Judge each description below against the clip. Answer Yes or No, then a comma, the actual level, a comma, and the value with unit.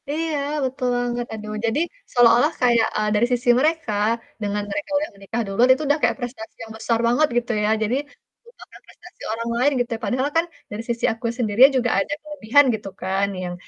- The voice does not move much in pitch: No, average, 3.7 semitones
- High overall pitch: Yes, high, 240 Hz